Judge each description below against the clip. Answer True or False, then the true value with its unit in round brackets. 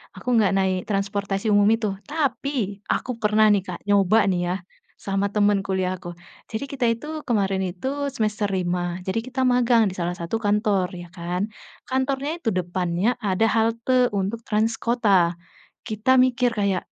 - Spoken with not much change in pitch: False (3.6 semitones)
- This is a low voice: False (205 Hz)